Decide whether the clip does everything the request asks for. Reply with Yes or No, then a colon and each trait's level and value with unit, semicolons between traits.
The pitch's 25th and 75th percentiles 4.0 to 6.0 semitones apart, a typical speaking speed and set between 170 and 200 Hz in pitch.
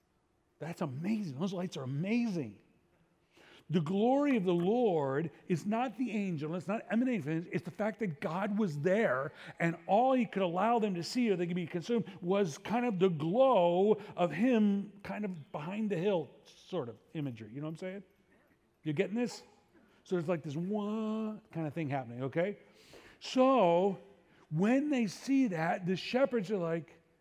Yes: average, 4.4 semitones; average, 180 wpm; high, 190 Hz